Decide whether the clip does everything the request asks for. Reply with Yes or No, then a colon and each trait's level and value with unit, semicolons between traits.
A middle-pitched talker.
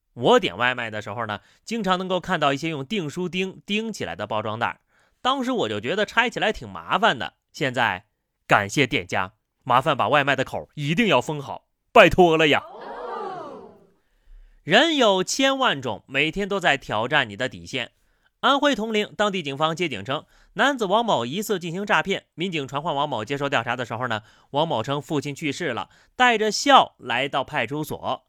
Yes: medium, 160 Hz